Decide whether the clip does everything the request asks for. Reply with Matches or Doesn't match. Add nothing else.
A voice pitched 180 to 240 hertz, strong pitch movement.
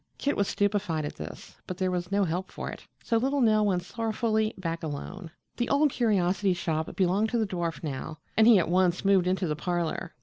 Doesn't match